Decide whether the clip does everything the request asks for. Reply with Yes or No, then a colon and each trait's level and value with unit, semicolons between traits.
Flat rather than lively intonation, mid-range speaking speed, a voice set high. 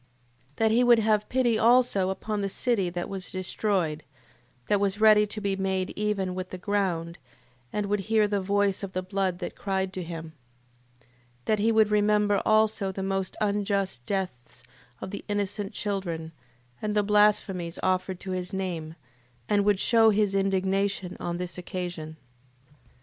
Yes: narrow, 2.2 semitones; average, 165 wpm; high, 195 Hz